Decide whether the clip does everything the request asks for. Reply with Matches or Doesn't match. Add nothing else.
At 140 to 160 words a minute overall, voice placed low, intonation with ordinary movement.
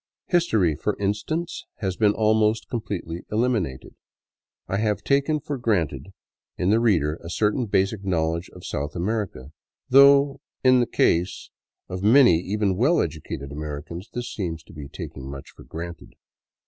Doesn't match